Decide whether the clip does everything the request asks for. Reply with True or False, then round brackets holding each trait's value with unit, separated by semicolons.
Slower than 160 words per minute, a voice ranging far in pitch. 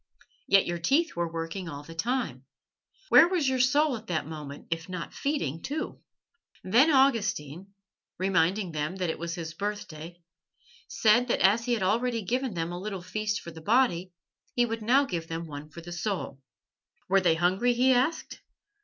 False (180 wpm; 6.6 semitones)